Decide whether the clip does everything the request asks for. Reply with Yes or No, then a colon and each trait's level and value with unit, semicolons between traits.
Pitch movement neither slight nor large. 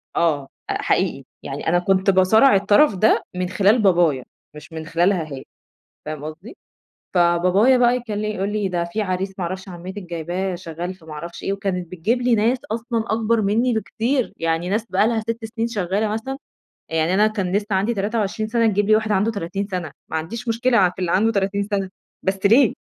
Yes: average, 3.8 semitones